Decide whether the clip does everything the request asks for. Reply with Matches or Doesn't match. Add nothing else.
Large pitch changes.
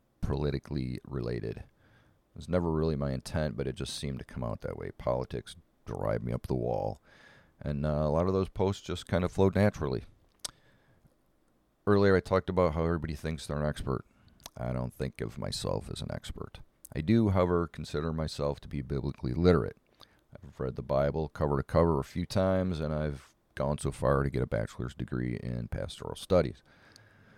Doesn't match